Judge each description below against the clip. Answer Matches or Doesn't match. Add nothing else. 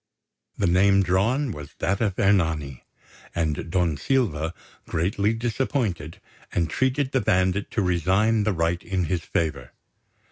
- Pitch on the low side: Matches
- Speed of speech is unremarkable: Doesn't match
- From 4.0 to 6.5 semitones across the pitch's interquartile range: Matches